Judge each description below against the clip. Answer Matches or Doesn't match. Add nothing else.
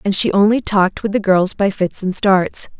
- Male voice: Doesn't match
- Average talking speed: Doesn't match